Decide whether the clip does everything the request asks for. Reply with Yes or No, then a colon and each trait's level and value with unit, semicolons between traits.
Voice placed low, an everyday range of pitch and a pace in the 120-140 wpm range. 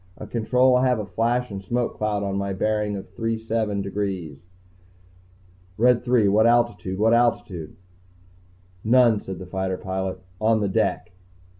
No: low, 105 Hz; average, 3.3 semitones; average, 155 wpm